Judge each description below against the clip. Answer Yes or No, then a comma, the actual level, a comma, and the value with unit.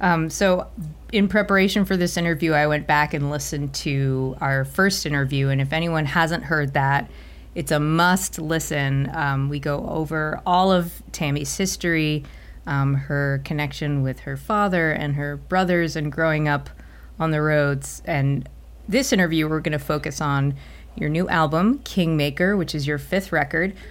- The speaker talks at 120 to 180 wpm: Yes, average, 165 wpm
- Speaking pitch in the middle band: Yes, medium, 155 Hz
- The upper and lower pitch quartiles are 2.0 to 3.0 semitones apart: No, average, 3.5 semitones